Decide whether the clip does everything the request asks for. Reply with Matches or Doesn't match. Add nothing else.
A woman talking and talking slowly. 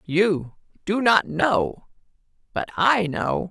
Doesn't match